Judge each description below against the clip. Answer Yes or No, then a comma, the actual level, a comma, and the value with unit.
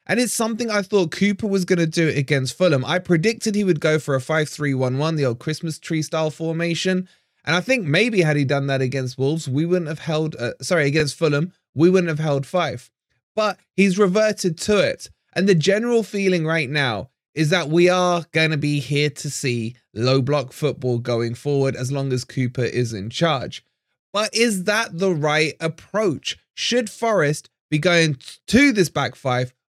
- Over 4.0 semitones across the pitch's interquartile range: Yes, average, 5.2 semitones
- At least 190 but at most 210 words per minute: Yes, average, 200 wpm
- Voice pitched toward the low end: No, medium, 160 Hz